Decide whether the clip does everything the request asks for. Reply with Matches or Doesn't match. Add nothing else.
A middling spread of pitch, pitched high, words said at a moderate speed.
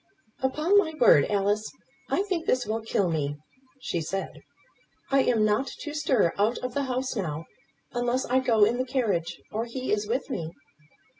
Matches